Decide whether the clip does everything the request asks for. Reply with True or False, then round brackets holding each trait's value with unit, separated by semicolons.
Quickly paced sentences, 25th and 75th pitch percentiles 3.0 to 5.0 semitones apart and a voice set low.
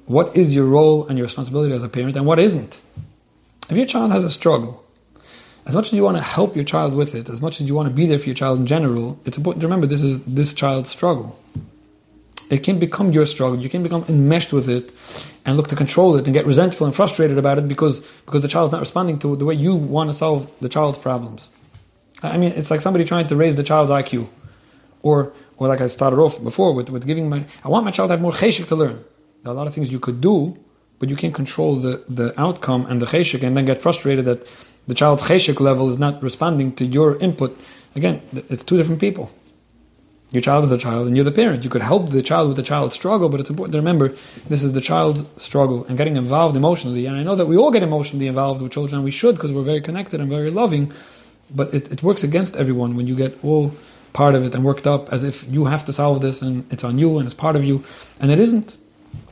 False (255 wpm; 3.4 semitones; 145 Hz)